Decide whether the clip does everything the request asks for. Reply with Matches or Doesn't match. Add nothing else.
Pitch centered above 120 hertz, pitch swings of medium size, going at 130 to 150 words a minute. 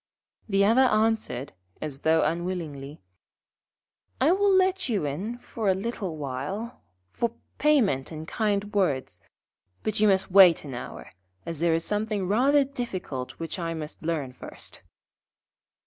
Doesn't match